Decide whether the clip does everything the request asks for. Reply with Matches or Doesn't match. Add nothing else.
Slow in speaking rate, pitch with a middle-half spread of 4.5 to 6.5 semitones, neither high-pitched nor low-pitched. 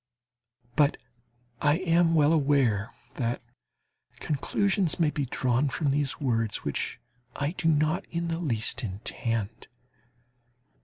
Matches